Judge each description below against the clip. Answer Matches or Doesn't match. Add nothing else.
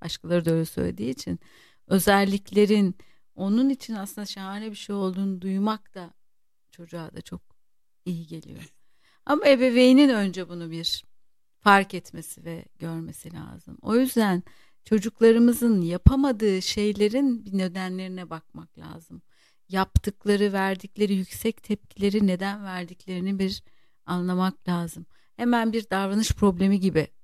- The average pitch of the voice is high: Matches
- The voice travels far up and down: Doesn't match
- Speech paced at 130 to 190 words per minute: Doesn't match